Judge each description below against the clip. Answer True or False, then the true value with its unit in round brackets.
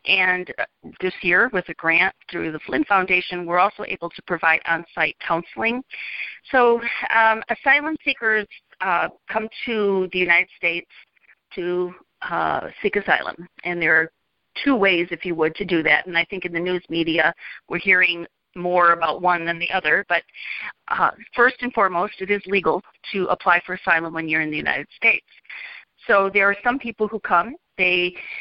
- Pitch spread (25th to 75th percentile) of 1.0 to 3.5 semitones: True (3.2 semitones)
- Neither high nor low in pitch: True (180 Hz)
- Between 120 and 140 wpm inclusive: False (175 wpm)